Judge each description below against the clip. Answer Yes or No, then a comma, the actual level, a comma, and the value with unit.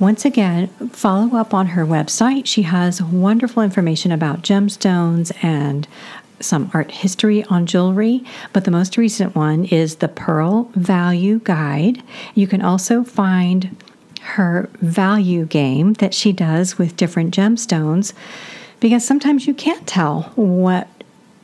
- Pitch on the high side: Yes, high, 195 Hz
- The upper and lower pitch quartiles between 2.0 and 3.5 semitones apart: No, average, 4.0 semitones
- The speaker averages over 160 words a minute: No, slow, 135 wpm